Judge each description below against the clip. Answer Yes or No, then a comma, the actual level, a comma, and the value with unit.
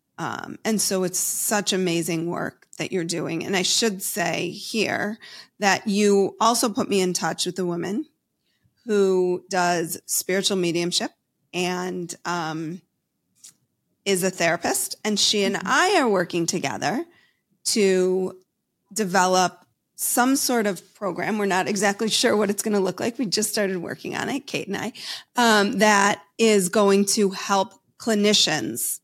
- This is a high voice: Yes, high, 195 Hz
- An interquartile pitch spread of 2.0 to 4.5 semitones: Yes, average, 2.8 semitones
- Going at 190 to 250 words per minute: No, average, 150 wpm